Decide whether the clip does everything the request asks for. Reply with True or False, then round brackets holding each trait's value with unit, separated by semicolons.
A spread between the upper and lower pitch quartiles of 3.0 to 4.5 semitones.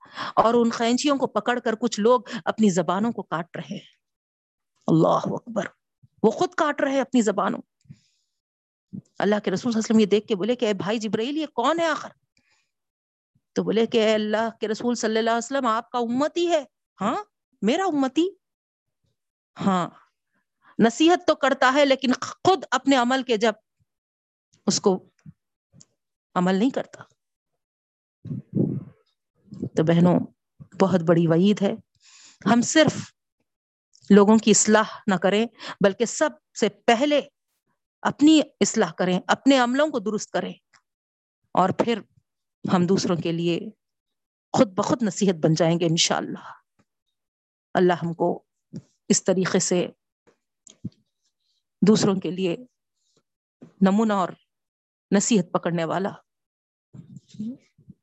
False (4.9 semitones)